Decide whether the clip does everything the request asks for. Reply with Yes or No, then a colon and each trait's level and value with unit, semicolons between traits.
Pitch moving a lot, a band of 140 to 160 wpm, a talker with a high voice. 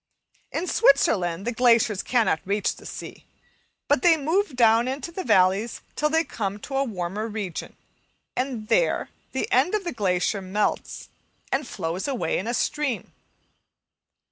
Yes: wide, 6.1 semitones; average, 150 wpm; high, 230 Hz